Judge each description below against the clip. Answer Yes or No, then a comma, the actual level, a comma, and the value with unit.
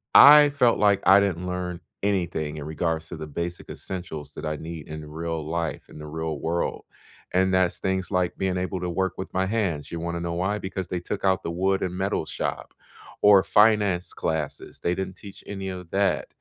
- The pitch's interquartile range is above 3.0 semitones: No, narrow, 2.6 semitones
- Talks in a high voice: No, very low, 90 Hz